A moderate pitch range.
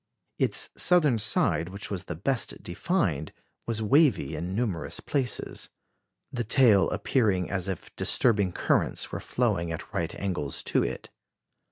No: wide, 5.7 semitones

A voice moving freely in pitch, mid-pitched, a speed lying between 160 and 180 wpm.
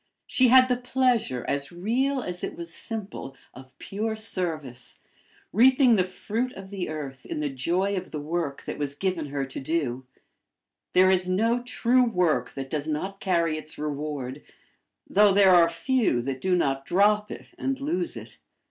Yes: wide, 7.0 semitones; medium, 180 Hz; average, 175 wpm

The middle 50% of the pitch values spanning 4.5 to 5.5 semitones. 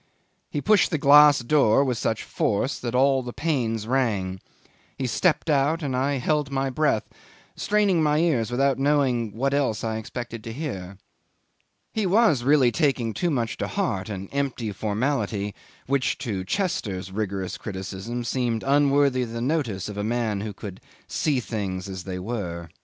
Yes: average, 5.1 semitones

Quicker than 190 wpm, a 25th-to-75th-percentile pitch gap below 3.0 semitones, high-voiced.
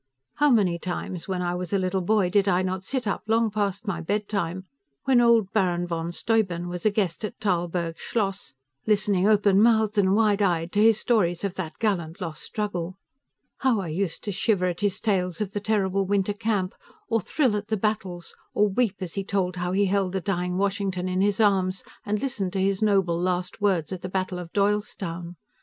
Yes: fast, 205 wpm; narrow, 2.6 semitones; high, 195 Hz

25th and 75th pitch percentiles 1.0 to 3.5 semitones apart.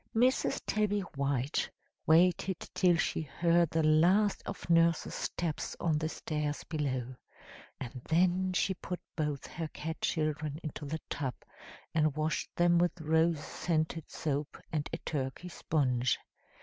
Yes: average, 2.7 semitones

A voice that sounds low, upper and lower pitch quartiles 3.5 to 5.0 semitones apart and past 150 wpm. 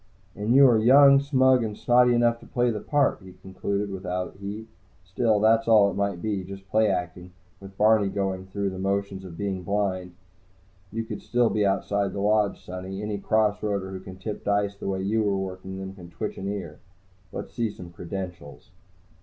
No: low, 100 Hz; narrow, 2.4 semitones; average, 195 wpm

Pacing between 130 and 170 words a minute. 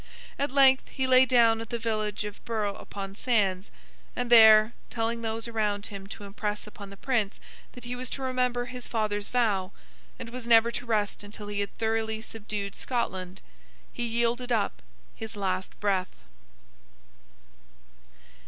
Yes: average, 155 wpm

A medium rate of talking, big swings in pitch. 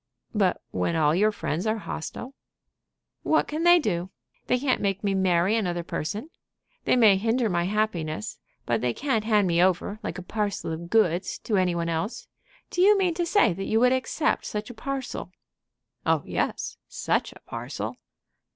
Yes: average, 180 wpm; wide, 5.9 semitones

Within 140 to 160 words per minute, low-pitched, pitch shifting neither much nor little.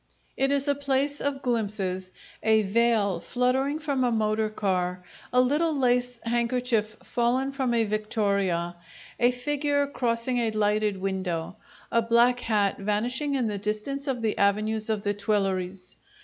No: average, 150 wpm; high, 230 Hz; average, 3.7 semitones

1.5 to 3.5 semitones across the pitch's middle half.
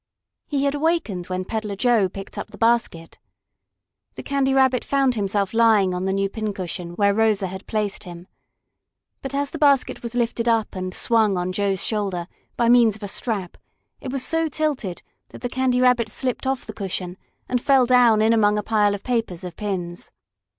No: average, 4.5 semitones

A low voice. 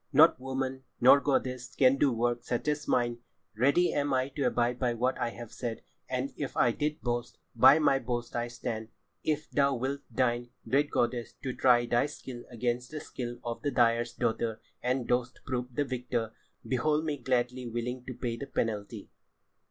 Yes: low, 125 Hz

